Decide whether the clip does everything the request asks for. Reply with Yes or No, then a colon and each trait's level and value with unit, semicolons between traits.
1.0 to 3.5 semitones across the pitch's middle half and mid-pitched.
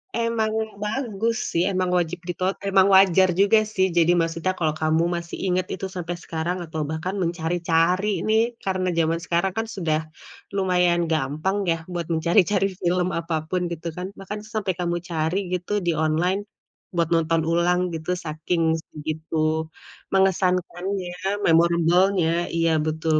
Yes: narrow, 2.6 semitones; medium, 175 Hz